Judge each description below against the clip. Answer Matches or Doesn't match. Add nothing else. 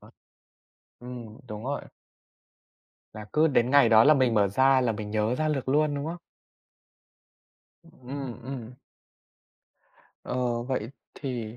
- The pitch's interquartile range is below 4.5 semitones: Matches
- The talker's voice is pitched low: Matches